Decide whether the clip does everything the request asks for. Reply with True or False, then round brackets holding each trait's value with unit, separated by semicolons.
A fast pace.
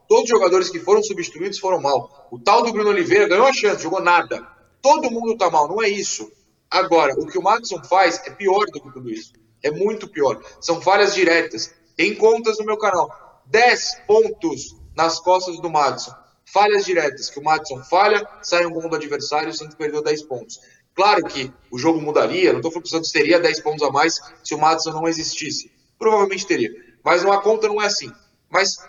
True (205 wpm)